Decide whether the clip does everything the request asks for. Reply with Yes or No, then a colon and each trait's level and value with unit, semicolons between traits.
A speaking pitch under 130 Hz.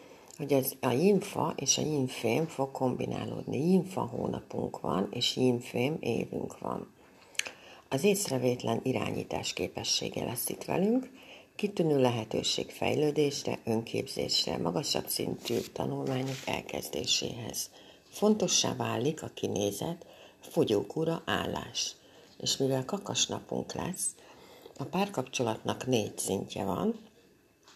No: medium, 140 Hz